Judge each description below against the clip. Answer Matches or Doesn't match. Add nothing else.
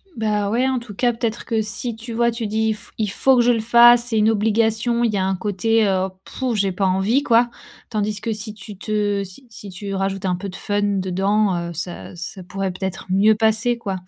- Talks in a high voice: Matches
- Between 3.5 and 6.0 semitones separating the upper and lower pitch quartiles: Doesn't match